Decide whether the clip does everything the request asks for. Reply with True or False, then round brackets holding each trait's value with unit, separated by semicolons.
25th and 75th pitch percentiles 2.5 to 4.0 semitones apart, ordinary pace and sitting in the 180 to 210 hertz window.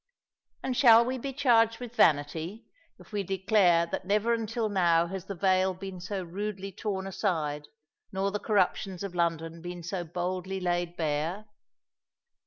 True (3.3 semitones; 155 wpm; 190 Hz)